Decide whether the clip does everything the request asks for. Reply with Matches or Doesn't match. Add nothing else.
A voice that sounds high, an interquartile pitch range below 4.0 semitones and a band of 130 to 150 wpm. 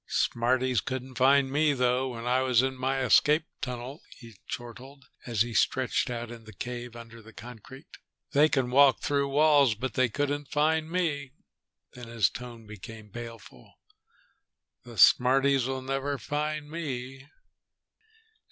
Doesn't match